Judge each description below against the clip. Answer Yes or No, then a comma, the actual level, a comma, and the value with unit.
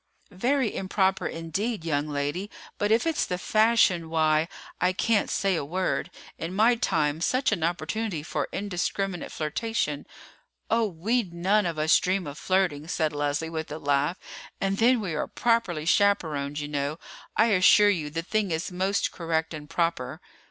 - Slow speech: No, average, 165 wpm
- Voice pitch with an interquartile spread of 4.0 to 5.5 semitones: Yes, average, 4.7 semitones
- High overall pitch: No, medium, 175 Hz